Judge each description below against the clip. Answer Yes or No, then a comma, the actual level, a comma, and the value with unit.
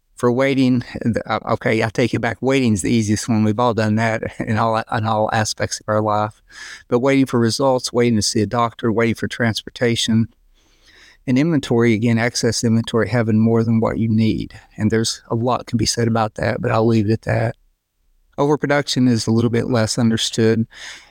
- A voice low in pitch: Yes, low, 115 Hz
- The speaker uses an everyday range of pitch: No, narrow, 1.6 semitones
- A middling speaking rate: Yes, average, 195 wpm